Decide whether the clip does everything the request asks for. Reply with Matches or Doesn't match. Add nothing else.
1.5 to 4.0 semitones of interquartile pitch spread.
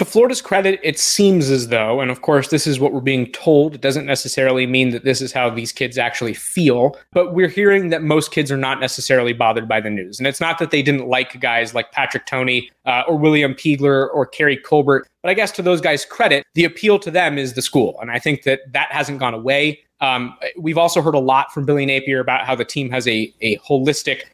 Matches